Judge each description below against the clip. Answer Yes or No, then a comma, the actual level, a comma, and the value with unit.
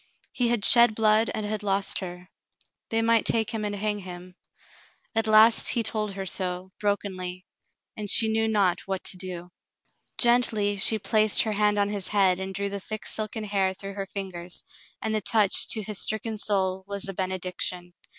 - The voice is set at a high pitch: Yes, high, 205 Hz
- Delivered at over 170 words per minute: Yes, average, 185 wpm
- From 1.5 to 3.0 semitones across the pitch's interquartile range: Yes, narrow, 2.4 semitones